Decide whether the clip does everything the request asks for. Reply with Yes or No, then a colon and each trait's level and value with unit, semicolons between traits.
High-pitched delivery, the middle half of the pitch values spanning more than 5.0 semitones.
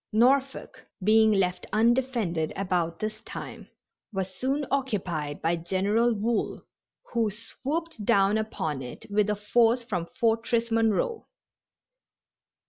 No: high, 215 Hz; average, 4.0 semitones